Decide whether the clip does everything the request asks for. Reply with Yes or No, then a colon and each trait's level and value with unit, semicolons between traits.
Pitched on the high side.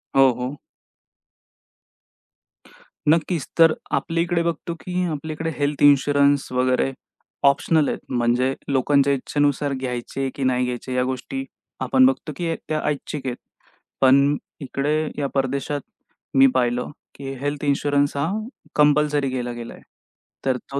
No: medium, 140 Hz